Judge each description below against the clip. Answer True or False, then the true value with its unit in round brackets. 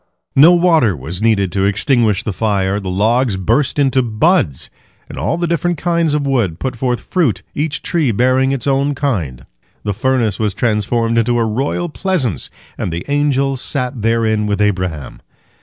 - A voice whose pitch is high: False (120 Hz)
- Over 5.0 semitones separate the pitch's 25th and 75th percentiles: True (5.4 semitones)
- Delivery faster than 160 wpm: True (175 wpm)